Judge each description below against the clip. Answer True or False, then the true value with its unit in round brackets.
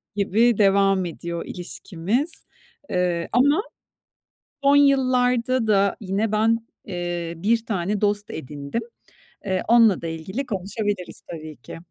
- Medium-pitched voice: False (200 Hz)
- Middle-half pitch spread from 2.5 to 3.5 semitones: False (4.8 semitones)